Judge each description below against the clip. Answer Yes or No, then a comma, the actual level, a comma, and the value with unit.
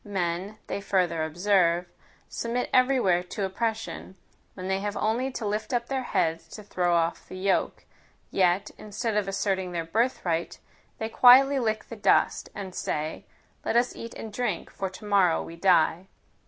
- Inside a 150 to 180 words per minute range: Yes, average, 165 wpm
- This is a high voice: Yes, high, 195 Hz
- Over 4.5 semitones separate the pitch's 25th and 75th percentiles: No, average, 4.0 semitones